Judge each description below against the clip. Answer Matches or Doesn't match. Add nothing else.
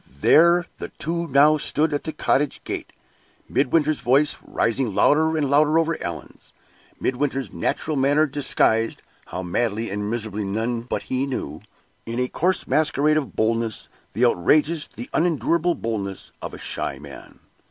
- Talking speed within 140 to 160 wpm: Matches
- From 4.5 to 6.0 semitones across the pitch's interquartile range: Matches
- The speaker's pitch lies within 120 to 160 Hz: Matches